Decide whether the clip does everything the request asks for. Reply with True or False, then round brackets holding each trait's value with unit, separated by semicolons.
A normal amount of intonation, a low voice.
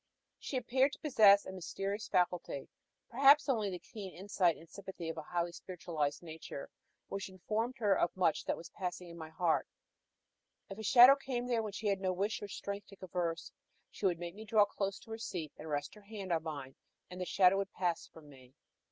False (3.9 semitones; 190 Hz)